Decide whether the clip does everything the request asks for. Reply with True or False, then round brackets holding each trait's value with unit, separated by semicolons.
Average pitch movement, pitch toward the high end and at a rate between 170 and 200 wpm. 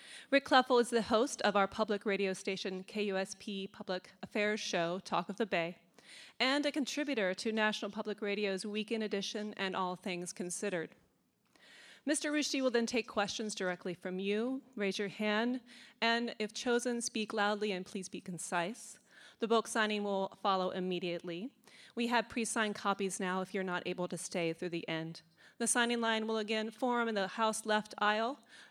True (3.5 semitones; 210 Hz; 175 wpm)